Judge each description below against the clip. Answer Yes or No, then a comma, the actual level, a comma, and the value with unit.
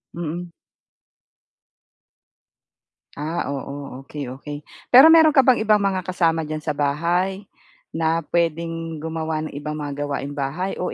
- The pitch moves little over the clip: No, average, 3.5 semitones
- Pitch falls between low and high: Yes, medium, 160 Hz